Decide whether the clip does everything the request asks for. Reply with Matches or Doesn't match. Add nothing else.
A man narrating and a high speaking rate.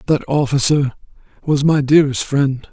Doesn't match